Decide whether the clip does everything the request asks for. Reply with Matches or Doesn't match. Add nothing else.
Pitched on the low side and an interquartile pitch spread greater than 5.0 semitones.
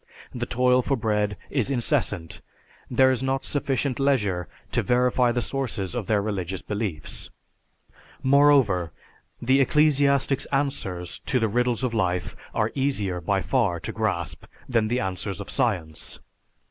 Matches